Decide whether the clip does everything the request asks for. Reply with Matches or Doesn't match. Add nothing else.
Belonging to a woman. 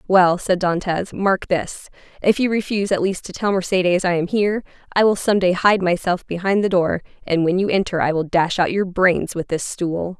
Matches